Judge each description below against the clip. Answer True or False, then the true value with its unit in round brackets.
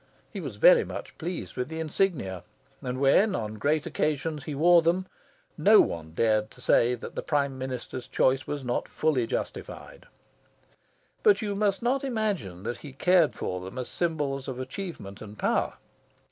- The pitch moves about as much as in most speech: False (6.6 semitones)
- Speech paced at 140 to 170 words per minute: True (165 wpm)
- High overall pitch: False (145 Hz)